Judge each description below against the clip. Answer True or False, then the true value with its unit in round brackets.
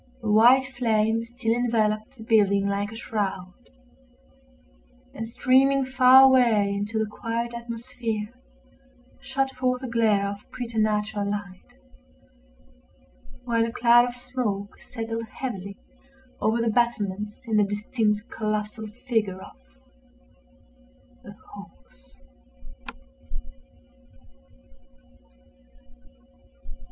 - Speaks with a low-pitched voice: False (225 Hz)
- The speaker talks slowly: True (95 wpm)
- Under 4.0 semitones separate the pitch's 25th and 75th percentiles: True (2.7 semitones)